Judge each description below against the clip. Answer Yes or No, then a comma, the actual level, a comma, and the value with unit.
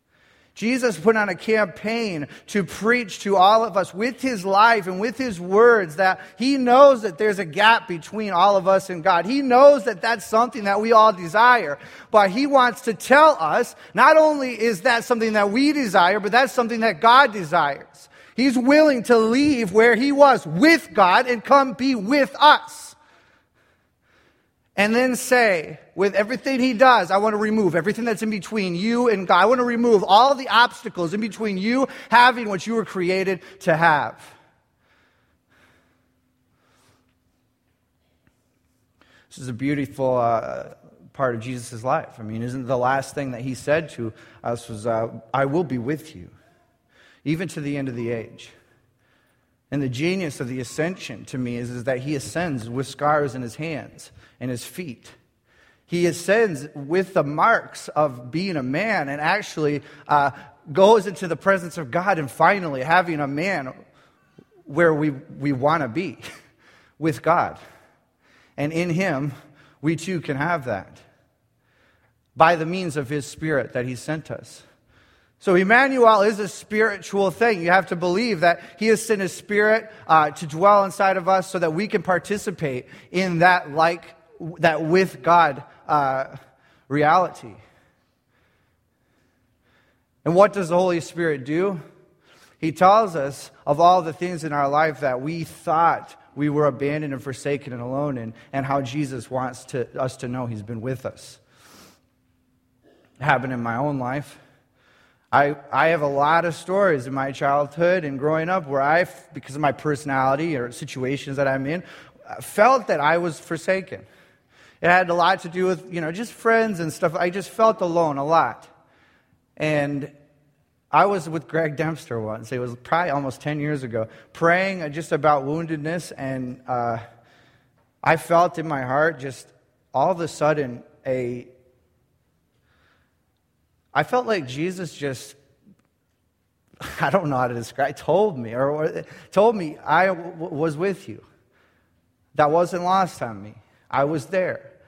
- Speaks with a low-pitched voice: No, medium, 165 Hz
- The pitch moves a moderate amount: No, wide, 6.6 semitones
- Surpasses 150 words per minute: Yes, average, 165 wpm